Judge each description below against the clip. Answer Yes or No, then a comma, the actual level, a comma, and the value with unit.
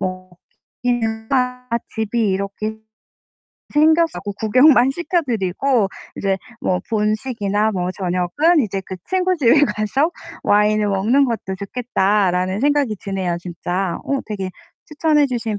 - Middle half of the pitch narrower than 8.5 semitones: Yes, wide, 5.4 semitones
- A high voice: Yes, high, 215 Hz